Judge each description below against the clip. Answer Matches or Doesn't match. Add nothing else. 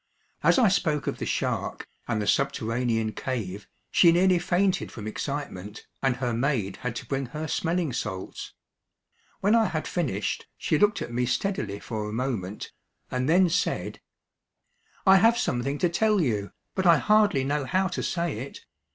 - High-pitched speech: Doesn't match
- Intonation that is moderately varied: Doesn't match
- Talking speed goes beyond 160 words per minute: Matches